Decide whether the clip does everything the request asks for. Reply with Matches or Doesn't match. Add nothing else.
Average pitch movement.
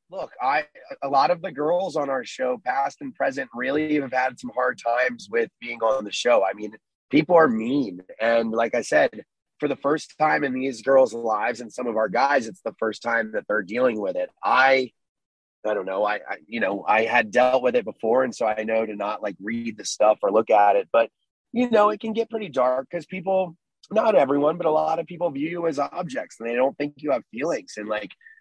Doesn't match